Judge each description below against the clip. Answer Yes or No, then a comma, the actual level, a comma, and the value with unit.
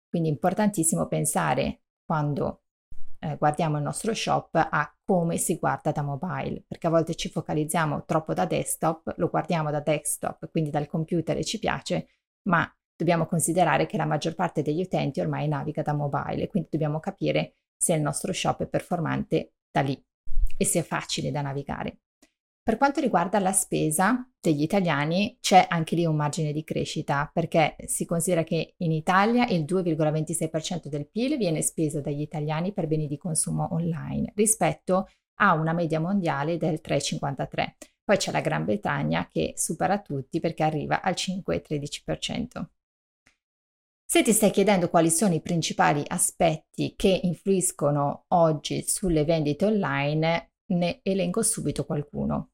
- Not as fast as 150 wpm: No, average, 155 wpm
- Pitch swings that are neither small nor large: Yes, average, 3.4 semitones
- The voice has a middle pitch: Yes, medium, 165 Hz